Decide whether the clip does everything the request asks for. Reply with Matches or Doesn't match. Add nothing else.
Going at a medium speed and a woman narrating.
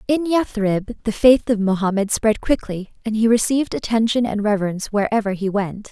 Matches